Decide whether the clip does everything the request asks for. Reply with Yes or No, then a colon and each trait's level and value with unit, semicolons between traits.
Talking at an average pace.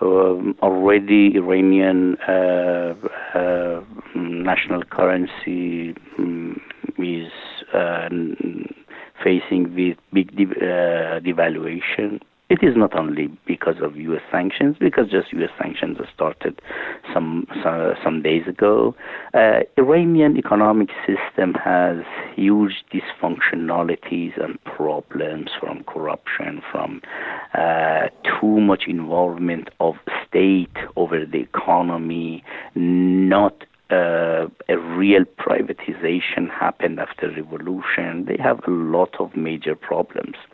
No: slow, 105 wpm